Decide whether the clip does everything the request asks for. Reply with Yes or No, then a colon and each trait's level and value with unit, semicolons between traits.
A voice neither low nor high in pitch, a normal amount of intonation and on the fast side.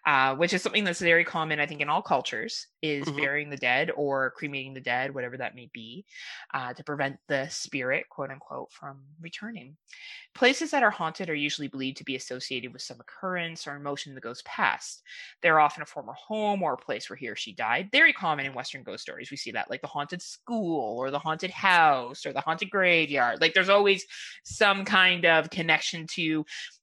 Yes: medium, 155 Hz; average, 4.7 semitones; fast, 210 wpm